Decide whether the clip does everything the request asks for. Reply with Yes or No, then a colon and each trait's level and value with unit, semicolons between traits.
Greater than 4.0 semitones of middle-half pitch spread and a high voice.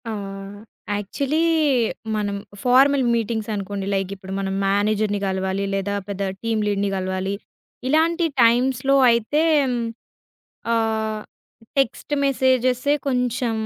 Yes: average, 4.4 semitones; high, 220 Hz